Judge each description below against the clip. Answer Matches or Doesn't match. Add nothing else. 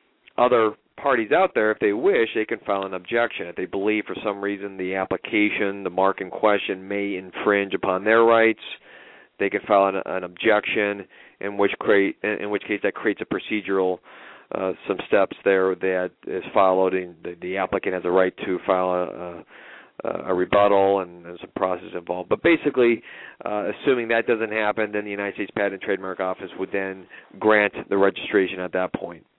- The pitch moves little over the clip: Matches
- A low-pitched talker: Matches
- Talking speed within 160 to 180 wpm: Doesn't match